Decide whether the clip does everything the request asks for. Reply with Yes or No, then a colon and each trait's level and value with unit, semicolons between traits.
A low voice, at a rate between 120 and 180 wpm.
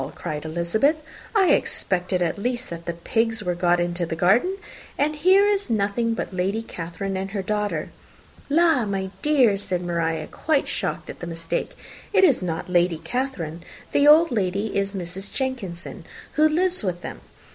No: high, 195 Hz; average, 170 wpm